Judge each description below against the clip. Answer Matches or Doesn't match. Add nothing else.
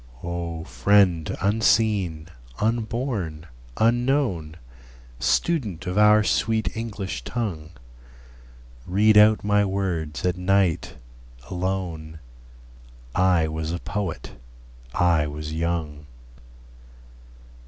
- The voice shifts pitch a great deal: Doesn't match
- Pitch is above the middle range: Doesn't match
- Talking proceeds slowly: Matches